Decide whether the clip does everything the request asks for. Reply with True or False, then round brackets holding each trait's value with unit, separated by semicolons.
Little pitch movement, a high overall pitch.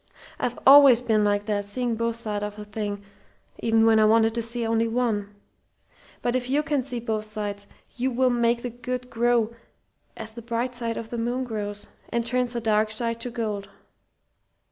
True (2.1 semitones; 230 Hz)